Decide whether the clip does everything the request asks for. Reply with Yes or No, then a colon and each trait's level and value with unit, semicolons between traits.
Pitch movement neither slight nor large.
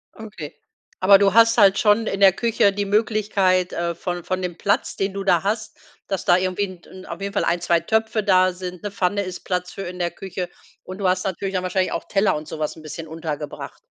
No: narrow, 2.2 semitones